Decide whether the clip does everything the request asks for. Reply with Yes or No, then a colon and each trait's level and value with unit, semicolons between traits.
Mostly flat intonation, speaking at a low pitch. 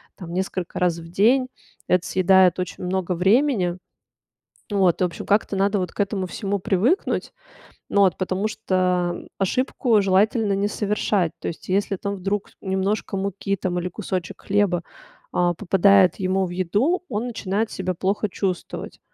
No: narrow, 2.1 semitones; high, 190 Hz